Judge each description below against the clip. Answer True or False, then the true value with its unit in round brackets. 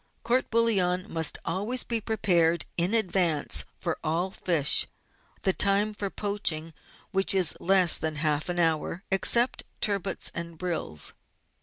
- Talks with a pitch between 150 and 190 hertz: True (185 Hz)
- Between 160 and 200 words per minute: False (135 wpm)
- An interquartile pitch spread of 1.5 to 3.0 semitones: False (3.5 semitones)